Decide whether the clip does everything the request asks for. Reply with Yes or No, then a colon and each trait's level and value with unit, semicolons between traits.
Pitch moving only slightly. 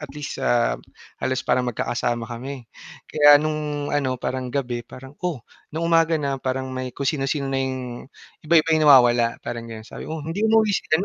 No: average, 3.6 semitones